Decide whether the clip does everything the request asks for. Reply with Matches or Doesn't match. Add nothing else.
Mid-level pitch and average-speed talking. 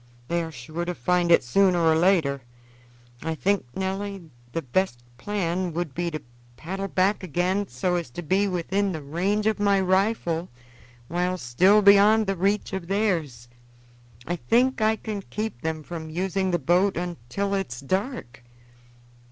Matches